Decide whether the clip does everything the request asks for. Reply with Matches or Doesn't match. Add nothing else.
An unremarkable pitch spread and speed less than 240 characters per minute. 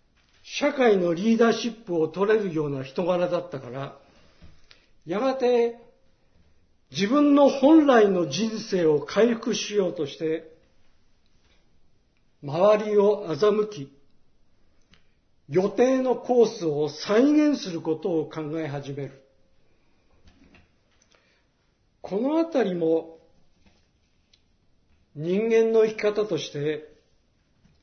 Doesn't match